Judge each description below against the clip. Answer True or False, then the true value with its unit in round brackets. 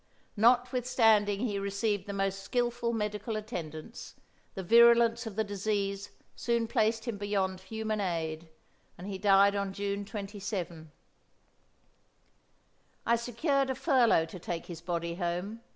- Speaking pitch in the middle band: False (205 Hz)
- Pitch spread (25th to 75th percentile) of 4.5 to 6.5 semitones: False (3.3 semitones)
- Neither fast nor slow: False (130 wpm)